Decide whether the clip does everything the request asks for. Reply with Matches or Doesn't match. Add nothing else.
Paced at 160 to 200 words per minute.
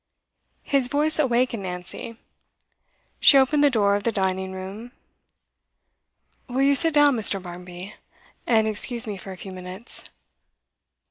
Doesn't match